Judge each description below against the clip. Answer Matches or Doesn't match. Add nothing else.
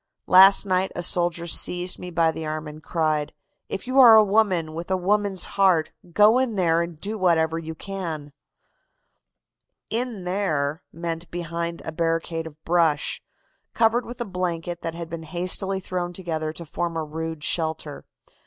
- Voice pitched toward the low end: Doesn't match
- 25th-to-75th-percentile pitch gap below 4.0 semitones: Matches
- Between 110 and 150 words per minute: Doesn't match